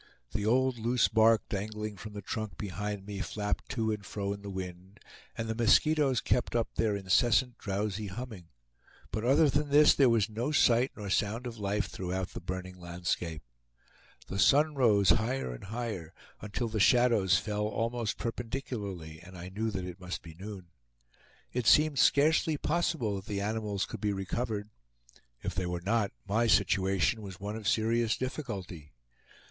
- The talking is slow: No, average, 170 wpm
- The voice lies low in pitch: Yes, low, 105 Hz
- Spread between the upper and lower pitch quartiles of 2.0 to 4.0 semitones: Yes, average, 3.6 semitones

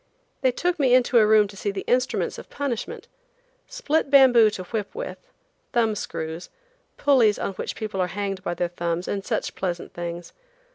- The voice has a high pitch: Yes, high, 210 Hz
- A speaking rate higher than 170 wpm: Yes, average, 180 wpm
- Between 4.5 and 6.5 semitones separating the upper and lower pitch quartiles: Yes, wide, 5.5 semitones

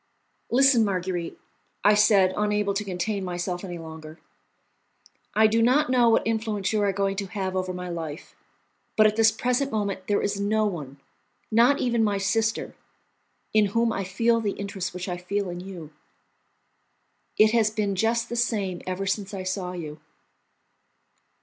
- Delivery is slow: No, average, 165 wpm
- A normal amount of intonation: Yes, average, 3.1 semitones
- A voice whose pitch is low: No, high, 200 Hz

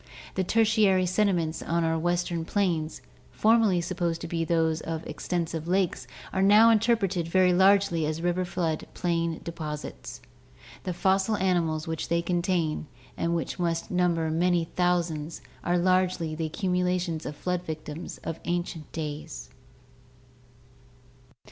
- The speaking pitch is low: No, medium, 175 Hz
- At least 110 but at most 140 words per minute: Yes, slow, 135 wpm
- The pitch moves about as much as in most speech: No, narrow, 2.2 semitones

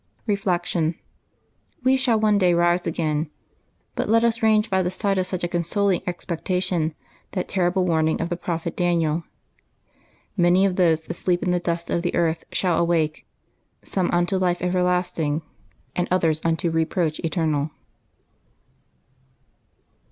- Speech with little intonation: Yes, narrow, 2.1 semitones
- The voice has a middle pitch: Yes, medium, 175 Hz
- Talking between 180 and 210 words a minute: No, average, 150 wpm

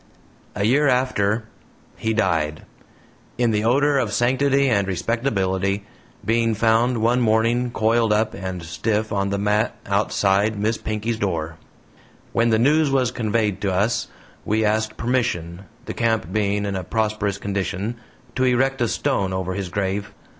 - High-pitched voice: No, low, 110 Hz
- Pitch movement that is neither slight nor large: Yes, average, 3.0 semitones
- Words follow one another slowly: No, average, 150 wpm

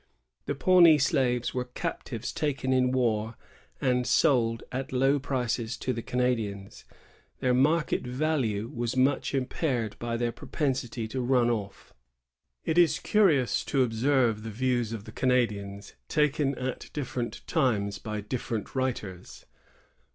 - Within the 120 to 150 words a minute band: Yes, slow, 135 wpm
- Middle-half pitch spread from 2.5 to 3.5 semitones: Yes, average, 2.9 semitones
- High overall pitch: No, low, 125 Hz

